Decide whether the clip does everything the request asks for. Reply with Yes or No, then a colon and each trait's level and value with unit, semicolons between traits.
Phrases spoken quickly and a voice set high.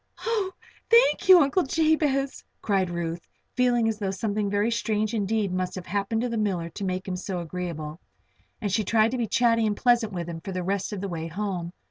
Yes: fast, 210 wpm; high, 205 Hz